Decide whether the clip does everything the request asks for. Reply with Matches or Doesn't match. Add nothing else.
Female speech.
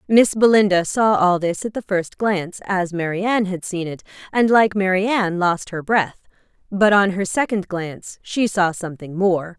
Matches